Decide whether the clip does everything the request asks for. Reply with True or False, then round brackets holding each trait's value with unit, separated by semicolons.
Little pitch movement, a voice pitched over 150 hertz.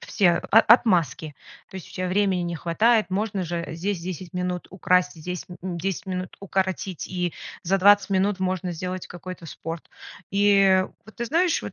True (2.1 semitones; 185 Hz)